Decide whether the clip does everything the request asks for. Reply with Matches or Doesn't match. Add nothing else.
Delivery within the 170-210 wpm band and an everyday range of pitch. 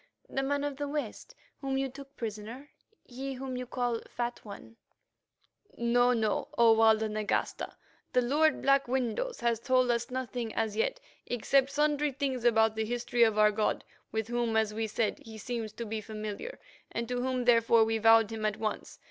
Matches